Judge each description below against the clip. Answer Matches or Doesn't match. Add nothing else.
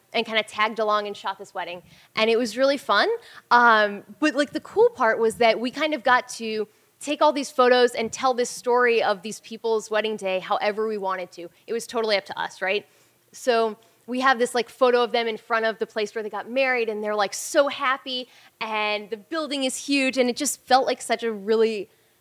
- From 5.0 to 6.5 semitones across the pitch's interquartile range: Doesn't match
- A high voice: Matches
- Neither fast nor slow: Doesn't match